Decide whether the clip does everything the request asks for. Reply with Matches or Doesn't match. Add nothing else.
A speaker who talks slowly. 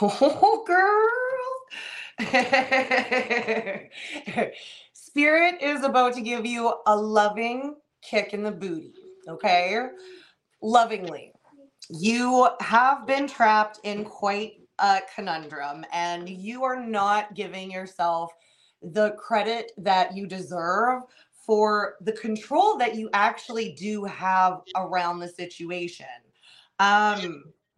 Matches